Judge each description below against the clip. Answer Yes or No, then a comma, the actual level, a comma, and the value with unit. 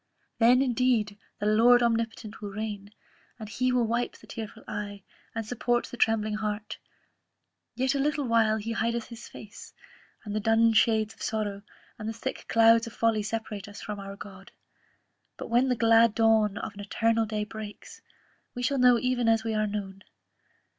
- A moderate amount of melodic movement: No, narrow, 1.8 semitones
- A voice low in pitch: No, high, 225 Hz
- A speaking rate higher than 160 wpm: Yes, average, 180 wpm